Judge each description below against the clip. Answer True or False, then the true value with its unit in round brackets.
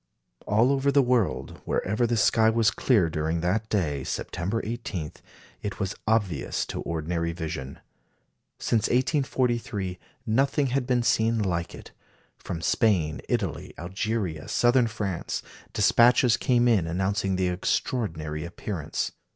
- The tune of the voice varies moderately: False (5.7 semitones)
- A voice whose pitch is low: True (105 Hz)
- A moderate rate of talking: False (130 wpm)